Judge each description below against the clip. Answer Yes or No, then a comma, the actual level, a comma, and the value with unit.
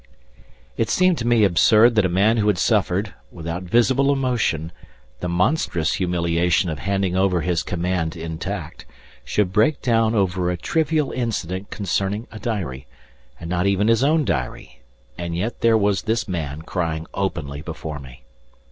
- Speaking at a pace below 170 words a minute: Yes, average, 155 wpm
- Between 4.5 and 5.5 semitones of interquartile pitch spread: Yes, average, 4.9 semitones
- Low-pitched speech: Yes, very low, 95 Hz